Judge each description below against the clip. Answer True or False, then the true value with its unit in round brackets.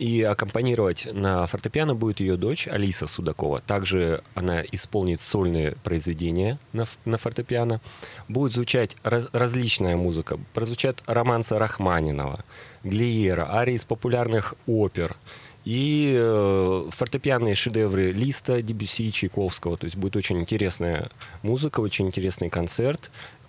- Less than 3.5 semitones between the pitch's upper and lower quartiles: False (4.3 semitones)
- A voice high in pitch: False (110 Hz)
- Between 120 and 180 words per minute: False (110 wpm)